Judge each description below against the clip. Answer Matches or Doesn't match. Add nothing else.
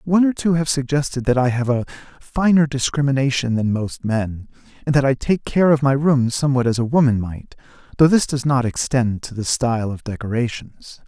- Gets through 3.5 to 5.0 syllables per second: Doesn't match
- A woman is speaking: Doesn't match